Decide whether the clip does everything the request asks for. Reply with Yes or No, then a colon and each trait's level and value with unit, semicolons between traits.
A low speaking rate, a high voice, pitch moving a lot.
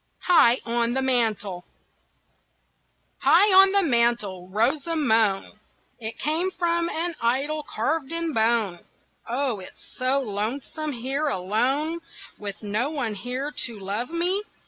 Yes: slow, 130 wpm; very high, 255 Hz; wide, 6.0 semitones